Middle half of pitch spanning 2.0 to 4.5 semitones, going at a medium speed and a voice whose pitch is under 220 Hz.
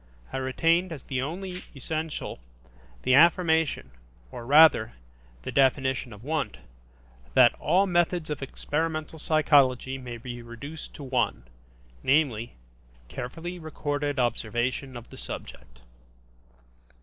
No: average, 4.1 semitones; slow, 115 wpm; medium, 140 Hz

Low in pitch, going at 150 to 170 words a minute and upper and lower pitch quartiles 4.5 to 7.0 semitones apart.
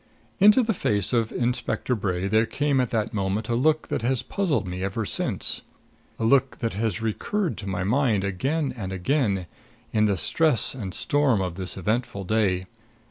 No: low, 110 Hz; average, 180 wpm; wide, 5.4 semitones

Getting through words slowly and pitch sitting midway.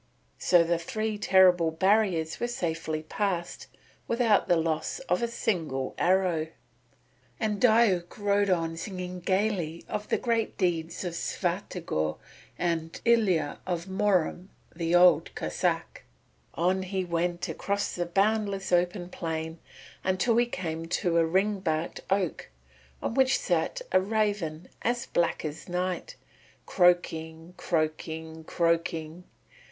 Yes: slow, 125 wpm; medium, 180 Hz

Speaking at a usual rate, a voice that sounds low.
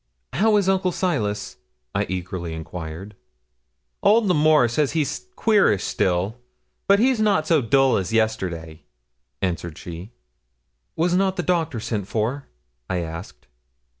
No: slow, 130 wpm; low, 120 Hz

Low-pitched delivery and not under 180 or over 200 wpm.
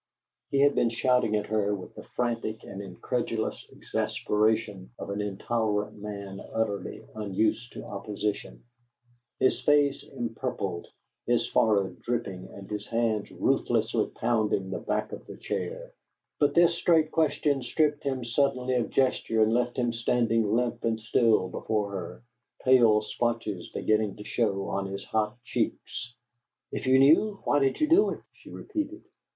No: low, 115 Hz; average, 150 wpm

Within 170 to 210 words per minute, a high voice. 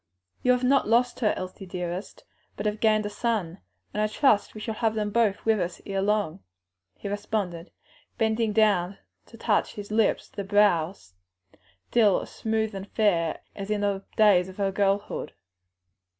Yes: average, 175 wpm; high, 205 Hz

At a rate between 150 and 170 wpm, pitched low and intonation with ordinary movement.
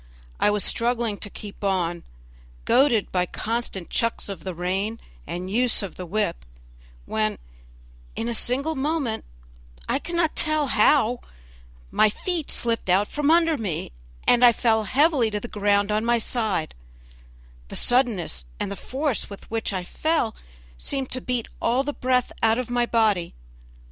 No: average, 155 wpm; high, 230 Hz; average, 4.2 semitones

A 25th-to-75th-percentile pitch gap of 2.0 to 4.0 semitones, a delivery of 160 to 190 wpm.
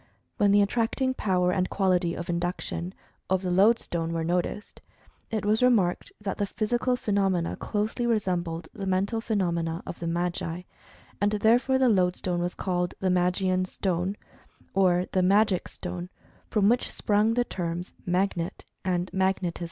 No: average, 2.9 semitones; average, 150 wpm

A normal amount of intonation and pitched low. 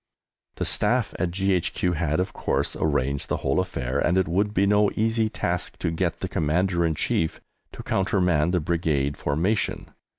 Yes: average, 3.6 semitones; very low, 85 Hz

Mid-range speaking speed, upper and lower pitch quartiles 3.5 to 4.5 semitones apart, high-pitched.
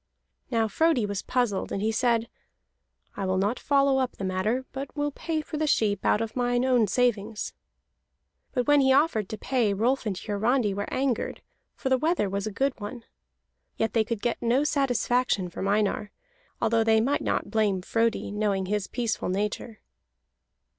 Yes: average, 175 wpm; average, 4.1 semitones; high, 230 Hz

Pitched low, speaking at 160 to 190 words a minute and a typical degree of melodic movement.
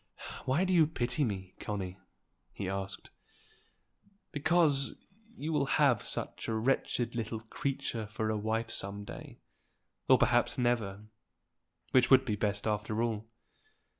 No: low, 115 Hz; slow, 135 wpm; average, 4.4 semitones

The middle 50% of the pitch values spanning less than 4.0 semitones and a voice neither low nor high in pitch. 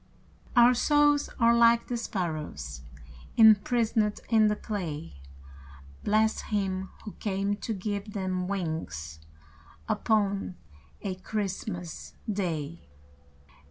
No: average, 3.6 semitones; high, 200 Hz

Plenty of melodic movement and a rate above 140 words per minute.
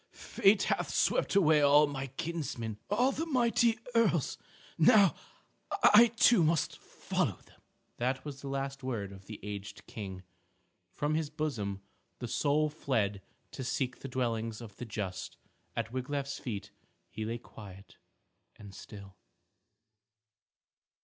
No: wide, 6.1 semitones; slow, 135 wpm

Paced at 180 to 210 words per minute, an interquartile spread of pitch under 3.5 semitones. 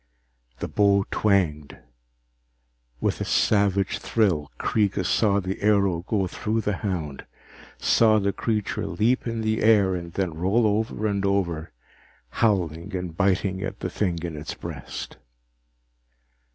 No: slow, 135 wpm; average, 2.9 semitones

